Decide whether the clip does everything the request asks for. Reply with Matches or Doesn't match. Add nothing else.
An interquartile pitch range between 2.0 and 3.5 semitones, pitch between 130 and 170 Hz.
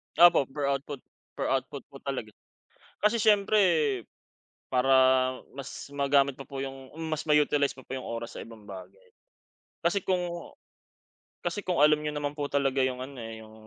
Matches